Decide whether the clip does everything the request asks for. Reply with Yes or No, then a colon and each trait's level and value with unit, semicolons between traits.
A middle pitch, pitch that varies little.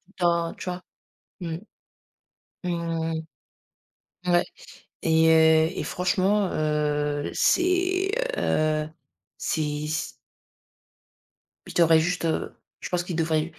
Yes: medium, 165 Hz; narrow, 2.1 semitones